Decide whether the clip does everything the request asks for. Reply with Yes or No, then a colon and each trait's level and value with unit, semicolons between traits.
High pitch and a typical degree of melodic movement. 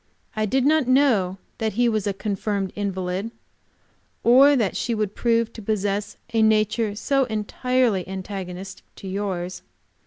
Yes: high, 215 Hz; average, 3.3 semitones